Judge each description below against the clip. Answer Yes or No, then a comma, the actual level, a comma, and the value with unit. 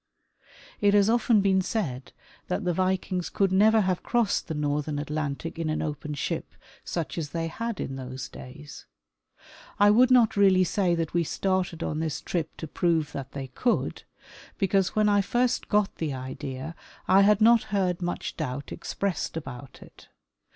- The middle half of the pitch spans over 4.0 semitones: Yes, average, 5.2 semitones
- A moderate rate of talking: Yes, average, 170 wpm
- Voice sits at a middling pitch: Yes, medium, 175 Hz